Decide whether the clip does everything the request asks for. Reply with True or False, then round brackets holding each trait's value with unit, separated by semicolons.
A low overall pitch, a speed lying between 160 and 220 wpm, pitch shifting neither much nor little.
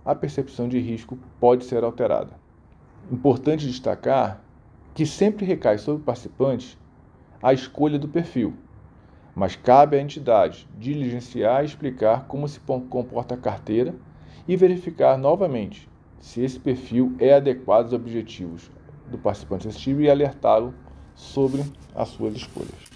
False (130 Hz; 130 wpm; 3.3 semitones)